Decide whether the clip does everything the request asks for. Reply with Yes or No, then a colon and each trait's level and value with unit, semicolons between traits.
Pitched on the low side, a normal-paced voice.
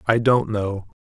Yes: low, 110 Hz; average, 175 wpm